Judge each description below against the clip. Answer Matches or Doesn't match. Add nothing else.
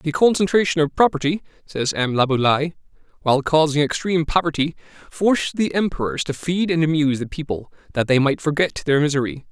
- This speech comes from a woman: Doesn't match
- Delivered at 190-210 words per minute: Doesn't match